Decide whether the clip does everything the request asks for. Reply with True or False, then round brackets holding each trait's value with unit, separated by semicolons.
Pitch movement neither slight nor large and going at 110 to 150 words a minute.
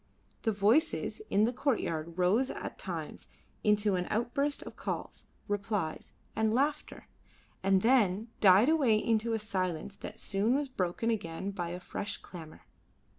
True (4.1 semitones; 145 wpm)